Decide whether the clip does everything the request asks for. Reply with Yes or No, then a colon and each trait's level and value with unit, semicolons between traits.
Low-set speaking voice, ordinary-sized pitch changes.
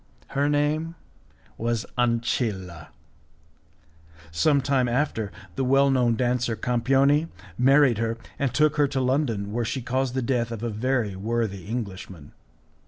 Yes: low, 125 Hz; average, 3.3 semitones